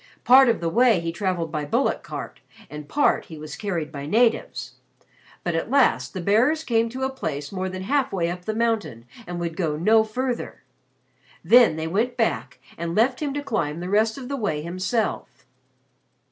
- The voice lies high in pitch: Yes, high, 195 Hz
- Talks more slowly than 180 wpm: No, average, 190 wpm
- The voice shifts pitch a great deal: Yes, wide, 6.3 semitones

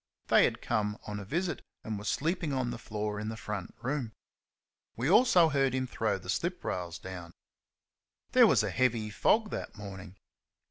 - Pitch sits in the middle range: No, low, 110 Hz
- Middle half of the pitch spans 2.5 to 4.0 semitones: No, wide, 5.5 semitones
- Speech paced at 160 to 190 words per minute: Yes, average, 180 wpm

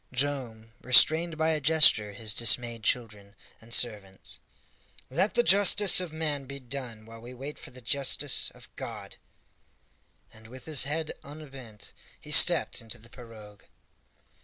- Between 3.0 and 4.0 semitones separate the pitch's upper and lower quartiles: No, average, 4.8 semitones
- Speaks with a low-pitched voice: Yes, low, 125 Hz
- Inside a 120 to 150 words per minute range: Yes, average, 145 wpm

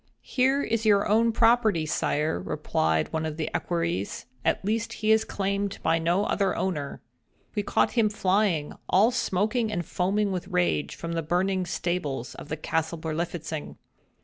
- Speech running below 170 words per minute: Yes, average, 160 wpm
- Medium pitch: Yes, medium, 180 Hz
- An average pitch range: Yes, average, 4.9 semitones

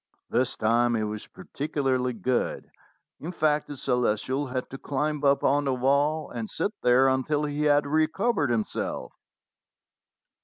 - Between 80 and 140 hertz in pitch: Yes, low, 135 Hz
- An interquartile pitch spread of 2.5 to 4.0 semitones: Yes, average, 3.1 semitones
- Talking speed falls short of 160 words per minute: Yes, average, 150 wpm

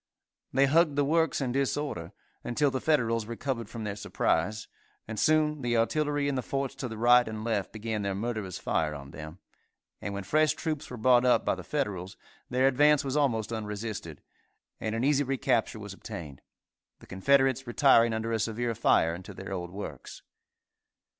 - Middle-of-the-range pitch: No, low, 115 Hz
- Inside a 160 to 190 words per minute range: Yes, average, 180 wpm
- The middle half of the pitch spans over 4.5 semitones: Yes, average, 5.0 semitones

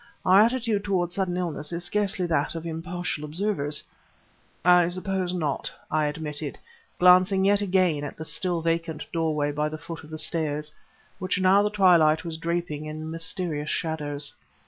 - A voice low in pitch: No, medium, 165 Hz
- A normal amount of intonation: Yes, average, 3.2 semitones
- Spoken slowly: No, average, 160 wpm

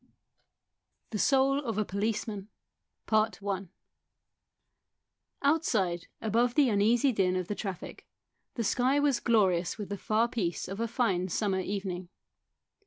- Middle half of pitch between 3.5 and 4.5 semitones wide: Yes, average, 4.0 semitones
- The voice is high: Yes, high, 215 Hz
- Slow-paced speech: Yes, slow, 120 wpm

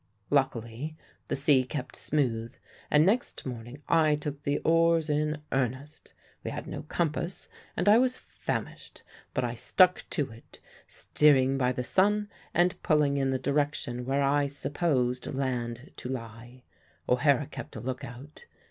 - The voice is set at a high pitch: No, medium, 140 Hz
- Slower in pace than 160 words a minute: Yes, average, 150 wpm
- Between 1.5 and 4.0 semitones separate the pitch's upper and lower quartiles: Yes, average, 3.3 semitones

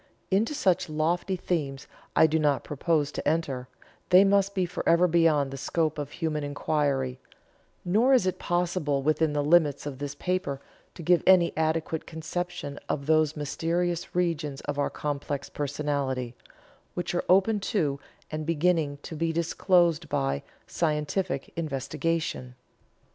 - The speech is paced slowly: No, average, 145 wpm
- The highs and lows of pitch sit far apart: No, average, 3.4 semitones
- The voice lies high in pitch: No, medium, 160 Hz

